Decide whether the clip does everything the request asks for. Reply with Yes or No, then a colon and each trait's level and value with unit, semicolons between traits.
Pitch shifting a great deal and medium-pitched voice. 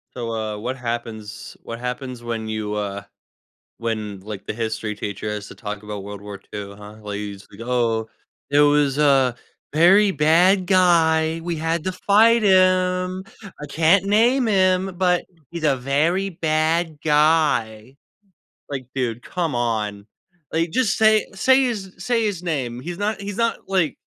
Yes: wide, 8.6 semitones; medium, 150 Hz